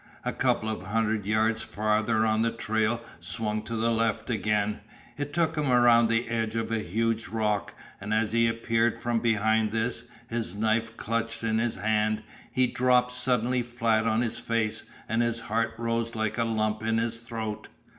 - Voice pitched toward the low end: Yes, low, 115 Hz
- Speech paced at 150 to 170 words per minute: No, average, 180 wpm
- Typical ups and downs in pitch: No, narrow, 1.2 semitones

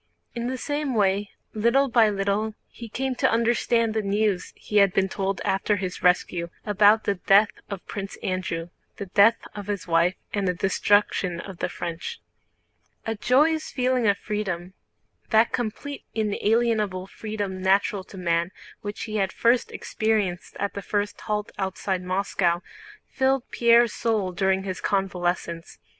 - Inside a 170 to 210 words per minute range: No, average, 150 wpm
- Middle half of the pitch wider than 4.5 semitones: No, average, 2.9 semitones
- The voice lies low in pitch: No, high, 205 Hz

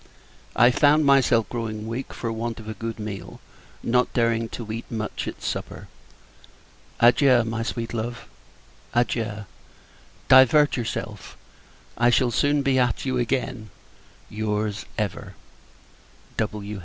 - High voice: No, low, 115 Hz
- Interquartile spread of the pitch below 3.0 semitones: Yes, narrow, 2.5 semitones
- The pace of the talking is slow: Yes, slow, 125 wpm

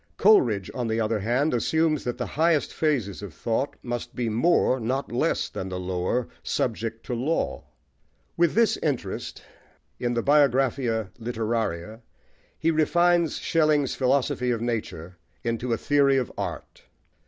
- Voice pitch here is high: No, low, 120 Hz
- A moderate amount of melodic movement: Yes, average, 4.4 semitones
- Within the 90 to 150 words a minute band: Yes, average, 140 wpm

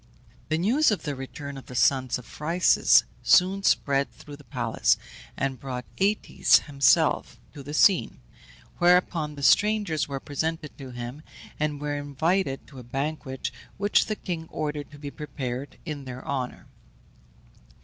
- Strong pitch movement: No, average, 3.4 semitones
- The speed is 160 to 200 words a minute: No, average, 150 wpm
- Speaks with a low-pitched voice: No, medium, 145 Hz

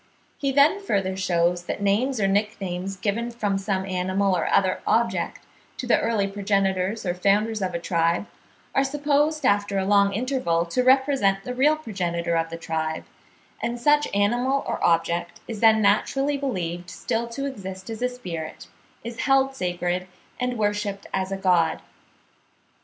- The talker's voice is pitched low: No, high, 200 Hz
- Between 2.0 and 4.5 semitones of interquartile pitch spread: No, average, 5.2 semitones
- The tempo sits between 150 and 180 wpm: Yes, average, 160 wpm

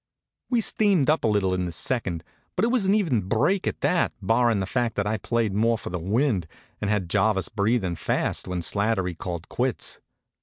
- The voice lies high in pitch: No, low, 110 Hz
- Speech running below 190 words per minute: No, average, 200 wpm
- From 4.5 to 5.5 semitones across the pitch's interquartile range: Yes, average, 5.1 semitones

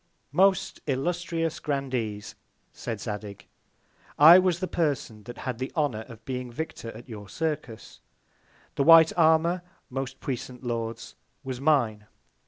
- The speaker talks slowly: Yes, slow, 130 wpm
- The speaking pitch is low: Yes, low, 130 Hz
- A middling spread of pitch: No, wide, 5.8 semitones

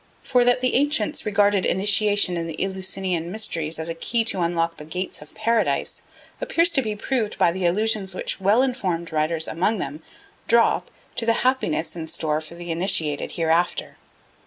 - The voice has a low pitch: No, high, 190 Hz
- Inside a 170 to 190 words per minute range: Yes, average, 175 wpm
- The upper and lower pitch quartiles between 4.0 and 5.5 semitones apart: Yes, average, 5.1 semitones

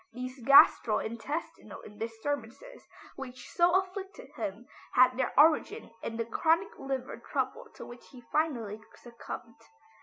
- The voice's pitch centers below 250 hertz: No, very high, 255 Hz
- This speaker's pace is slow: Yes, slow, 125 wpm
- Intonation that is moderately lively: No, wide, 5.8 semitones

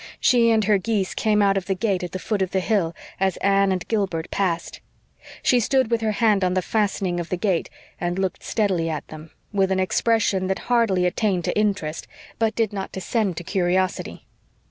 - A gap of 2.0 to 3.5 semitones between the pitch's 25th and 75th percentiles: Yes, average, 2.9 semitones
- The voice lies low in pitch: No, high, 195 Hz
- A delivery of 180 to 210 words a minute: Yes, fast, 205 wpm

